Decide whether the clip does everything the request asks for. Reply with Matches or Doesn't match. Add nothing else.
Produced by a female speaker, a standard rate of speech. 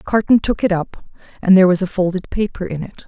Doesn't match